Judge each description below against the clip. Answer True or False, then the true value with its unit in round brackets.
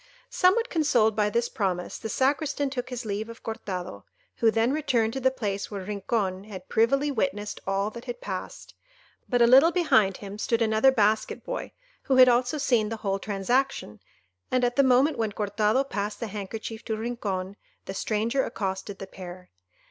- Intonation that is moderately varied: True (4.1 semitones)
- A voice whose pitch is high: True (225 Hz)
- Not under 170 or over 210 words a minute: True (180 wpm)